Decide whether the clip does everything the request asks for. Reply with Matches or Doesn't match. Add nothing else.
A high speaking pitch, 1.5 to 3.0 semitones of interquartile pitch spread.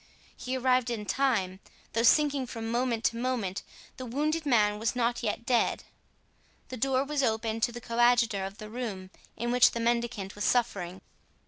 Matches